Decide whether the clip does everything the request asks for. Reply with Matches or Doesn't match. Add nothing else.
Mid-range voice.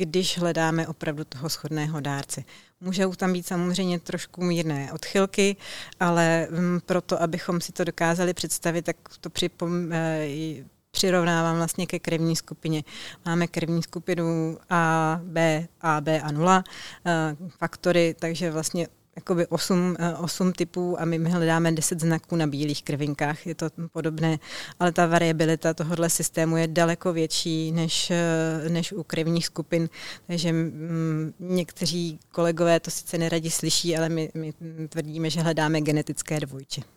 Matches